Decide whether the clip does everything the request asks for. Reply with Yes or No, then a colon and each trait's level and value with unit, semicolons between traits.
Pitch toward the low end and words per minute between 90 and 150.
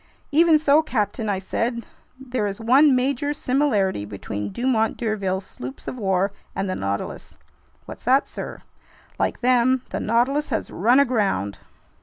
No: high, 235 Hz; average, 145 wpm